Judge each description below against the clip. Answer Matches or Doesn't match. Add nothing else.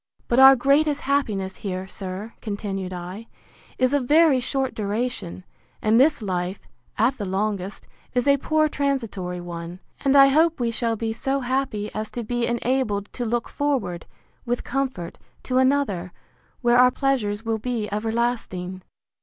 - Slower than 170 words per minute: Matches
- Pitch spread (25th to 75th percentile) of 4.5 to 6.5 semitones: Matches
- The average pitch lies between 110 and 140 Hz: Doesn't match